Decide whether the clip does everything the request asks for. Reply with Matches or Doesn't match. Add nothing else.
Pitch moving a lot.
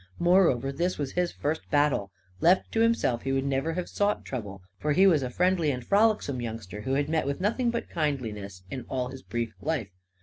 Matches